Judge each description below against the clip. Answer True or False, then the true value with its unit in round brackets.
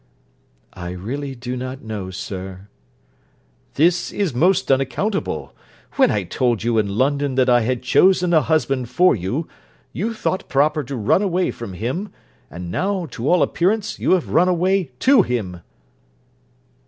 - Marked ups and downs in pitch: True (8.1 semitones)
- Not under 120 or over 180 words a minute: True (155 wpm)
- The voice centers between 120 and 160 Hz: True (135 Hz)